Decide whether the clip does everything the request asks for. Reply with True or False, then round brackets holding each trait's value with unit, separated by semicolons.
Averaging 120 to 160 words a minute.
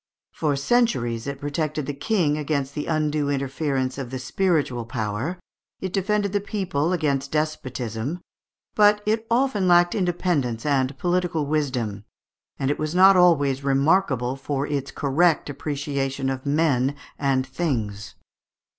True (135 wpm)